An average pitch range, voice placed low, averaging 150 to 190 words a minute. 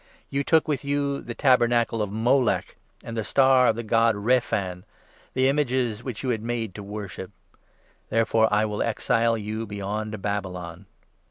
Yes: average, 3.3 semitones; low, 115 Hz; average, 170 wpm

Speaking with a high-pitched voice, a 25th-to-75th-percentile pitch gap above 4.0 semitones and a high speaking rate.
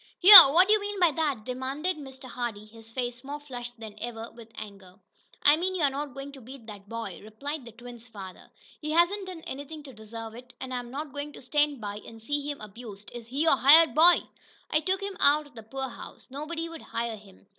Yes: very high, 265 Hz; average, 4.9 semitones; fast, 220 wpm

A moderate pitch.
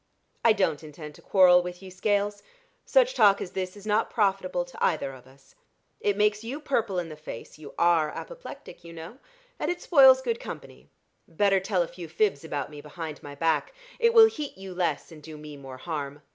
Yes: medium, 180 Hz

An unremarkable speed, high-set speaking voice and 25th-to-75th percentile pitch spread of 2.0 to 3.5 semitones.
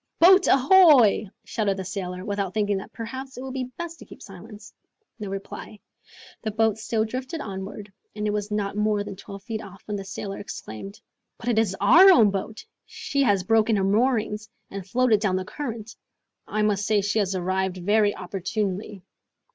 Yes: average, 185 wpm; high, 210 Hz; narrow, 2.5 semitones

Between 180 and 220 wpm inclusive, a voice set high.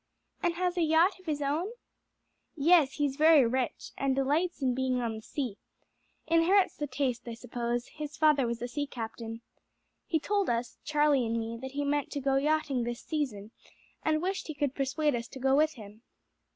Yes: average, 190 wpm; very high, 280 Hz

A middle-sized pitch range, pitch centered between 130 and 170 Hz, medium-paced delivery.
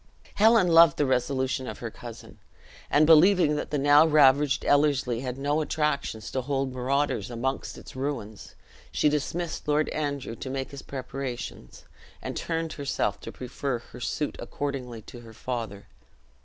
Yes: average, 3.0 semitones; medium, 140 Hz; average, 155 wpm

